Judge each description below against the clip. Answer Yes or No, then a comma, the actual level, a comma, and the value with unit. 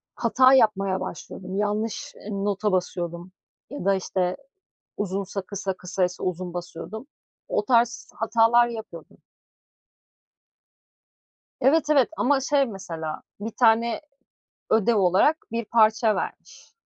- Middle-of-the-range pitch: No, high, 210 Hz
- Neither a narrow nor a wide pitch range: Yes, average, 4.0 semitones